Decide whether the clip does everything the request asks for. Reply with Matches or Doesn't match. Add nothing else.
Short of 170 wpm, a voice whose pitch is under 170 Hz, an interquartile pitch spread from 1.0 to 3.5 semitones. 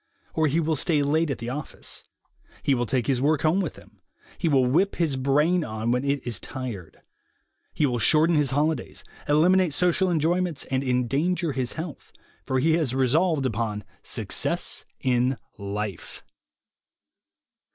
Doesn't match